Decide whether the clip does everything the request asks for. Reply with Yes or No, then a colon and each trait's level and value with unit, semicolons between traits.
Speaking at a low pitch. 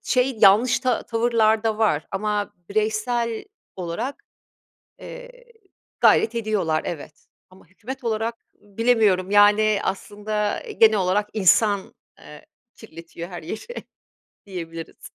No: high, 210 Hz